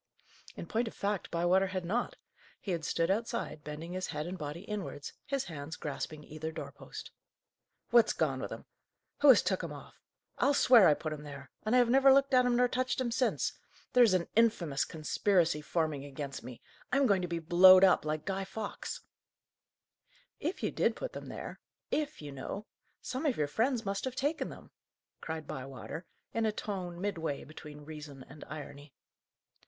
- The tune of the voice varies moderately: No, wide, 7.2 semitones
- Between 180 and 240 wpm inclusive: Yes, average, 185 wpm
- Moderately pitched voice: Yes, medium, 180 Hz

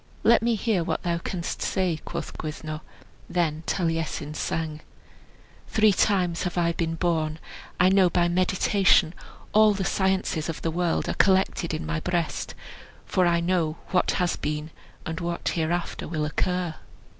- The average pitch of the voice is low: No, medium, 170 Hz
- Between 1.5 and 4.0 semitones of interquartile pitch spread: Yes, narrow, 2.4 semitones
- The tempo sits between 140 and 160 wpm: Yes, average, 155 wpm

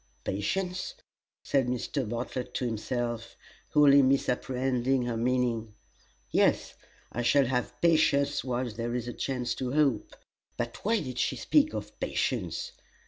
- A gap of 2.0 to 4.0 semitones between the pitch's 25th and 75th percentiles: Yes, average, 2.8 semitones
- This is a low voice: Yes, low, 125 Hz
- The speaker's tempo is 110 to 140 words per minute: Yes, slow, 135 wpm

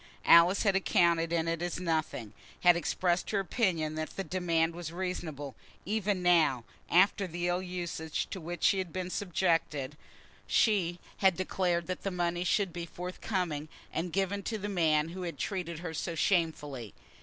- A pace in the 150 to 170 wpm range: Yes, average, 165 wpm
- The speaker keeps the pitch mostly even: Yes, narrow, 2.3 semitones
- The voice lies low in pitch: No, medium, 175 Hz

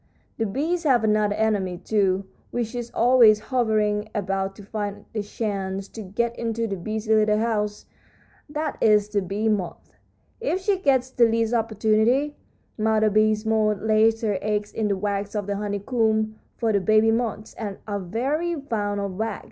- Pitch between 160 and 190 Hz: No, high, 215 Hz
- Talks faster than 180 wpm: No, average, 165 wpm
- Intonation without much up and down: Yes, narrow, 2.0 semitones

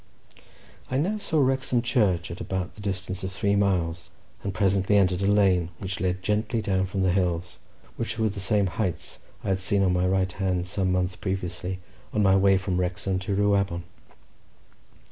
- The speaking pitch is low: Yes, very low, 95 Hz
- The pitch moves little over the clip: Yes, narrow, 1.8 semitones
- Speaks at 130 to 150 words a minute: No, average, 185 wpm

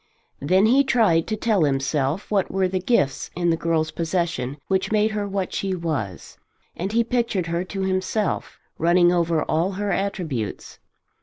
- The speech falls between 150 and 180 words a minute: Yes, average, 165 wpm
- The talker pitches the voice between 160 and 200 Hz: Yes, medium, 185 Hz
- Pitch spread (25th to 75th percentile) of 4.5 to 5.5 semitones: No, average, 3.7 semitones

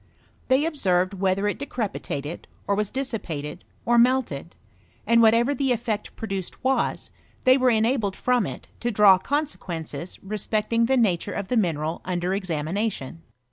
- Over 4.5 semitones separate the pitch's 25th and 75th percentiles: Yes, average, 4.9 semitones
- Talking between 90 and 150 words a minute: Yes, average, 145 wpm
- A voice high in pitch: Yes, high, 210 Hz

